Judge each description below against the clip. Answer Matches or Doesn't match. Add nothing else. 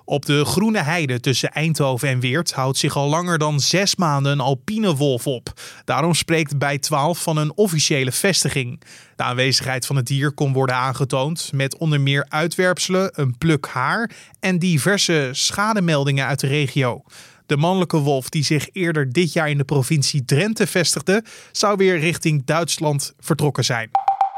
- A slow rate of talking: Doesn't match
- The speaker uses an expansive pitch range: Doesn't match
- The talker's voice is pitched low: Doesn't match